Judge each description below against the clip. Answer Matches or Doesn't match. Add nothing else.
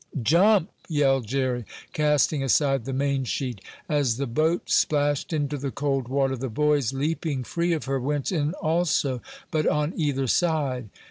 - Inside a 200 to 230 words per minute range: Doesn't match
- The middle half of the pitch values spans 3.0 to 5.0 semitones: Doesn't match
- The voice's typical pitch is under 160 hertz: Matches